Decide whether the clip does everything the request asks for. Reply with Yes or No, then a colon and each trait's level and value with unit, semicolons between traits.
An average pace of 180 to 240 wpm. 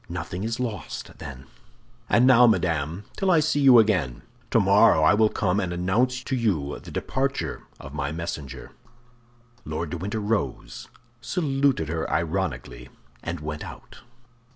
No: average, 145 wpm